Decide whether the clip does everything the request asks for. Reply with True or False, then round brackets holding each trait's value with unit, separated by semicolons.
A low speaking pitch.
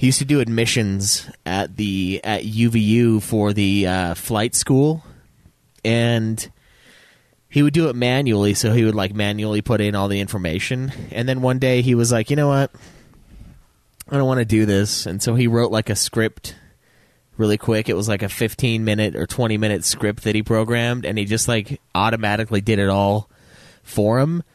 True (110 Hz)